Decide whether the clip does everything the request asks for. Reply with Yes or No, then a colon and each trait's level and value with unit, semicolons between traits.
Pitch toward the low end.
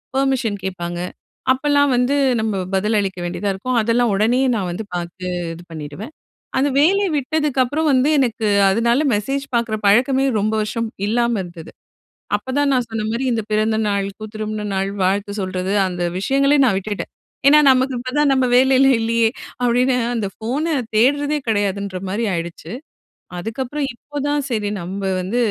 No: high, 230 Hz